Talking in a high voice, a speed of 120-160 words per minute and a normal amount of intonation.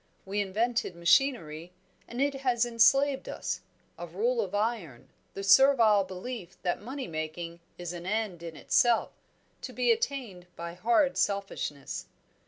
No: high, 205 Hz; average, 140 wpm; wide, 6.3 semitones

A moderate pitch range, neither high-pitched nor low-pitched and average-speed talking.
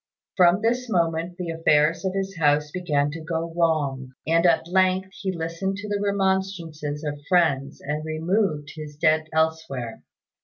Yes: average, 3.8 semitones; medium, 165 Hz; average, 155 wpm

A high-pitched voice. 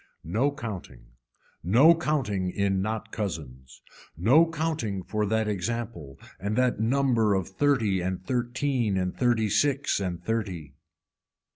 No: low, 110 Hz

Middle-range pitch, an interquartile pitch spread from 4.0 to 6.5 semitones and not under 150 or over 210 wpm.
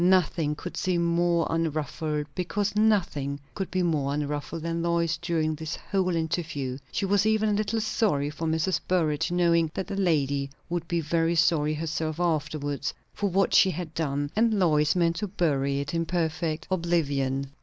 No: medium, 165 Hz; average, 3.1 semitones; average, 170 wpm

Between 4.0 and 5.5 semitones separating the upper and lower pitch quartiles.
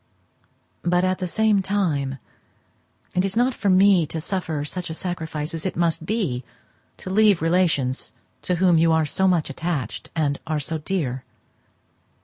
No: average, 3.4 semitones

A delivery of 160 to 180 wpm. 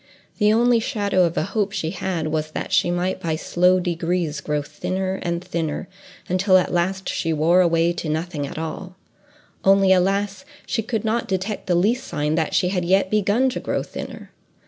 No: average, 190 wpm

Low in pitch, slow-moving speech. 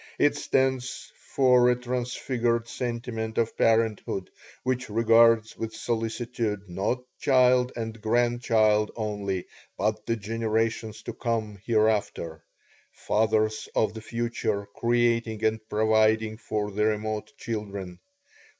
Yes: low, 110 Hz; slow, 110 wpm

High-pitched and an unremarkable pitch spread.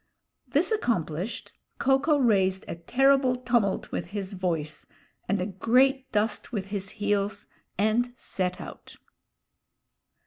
Yes: high, 210 Hz; average, 5.0 semitones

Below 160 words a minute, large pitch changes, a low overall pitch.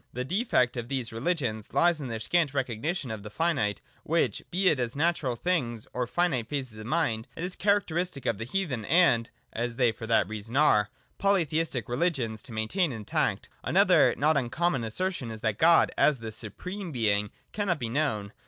No: average, 190 wpm; wide, 7.0 semitones; low, 130 Hz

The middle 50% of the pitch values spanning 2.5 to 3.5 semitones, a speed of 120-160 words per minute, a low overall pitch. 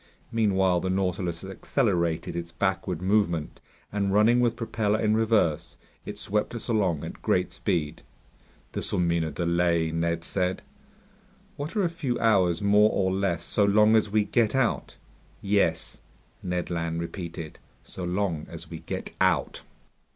No: average, 4.0 semitones; average, 150 wpm; very low, 95 Hz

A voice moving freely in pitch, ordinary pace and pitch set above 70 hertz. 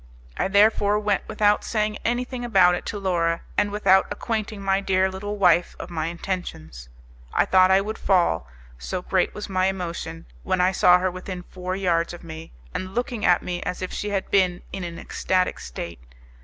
No: narrow, 2.5 semitones; average, 190 wpm; medium, 185 Hz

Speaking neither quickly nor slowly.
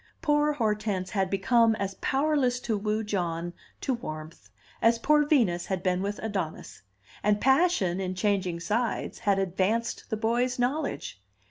Yes: average, 145 wpm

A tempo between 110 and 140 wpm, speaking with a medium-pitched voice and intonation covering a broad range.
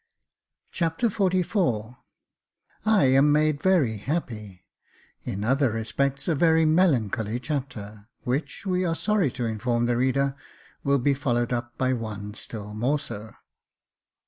No: slow, 135 wpm; low, 130 Hz; wide, 5.7 semitones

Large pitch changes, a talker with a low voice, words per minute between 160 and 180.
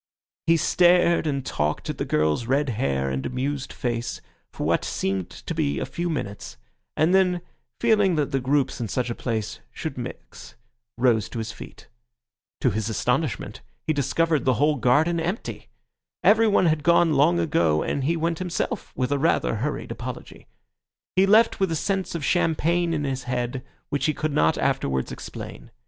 No: wide, 5.8 semitones; medium, 145 Hz; average, 175 wpm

